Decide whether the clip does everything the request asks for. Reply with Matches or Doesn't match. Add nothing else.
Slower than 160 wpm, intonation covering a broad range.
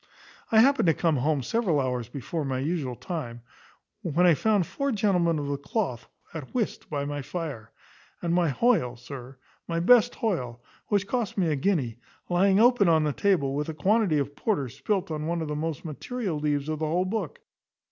Doesn't match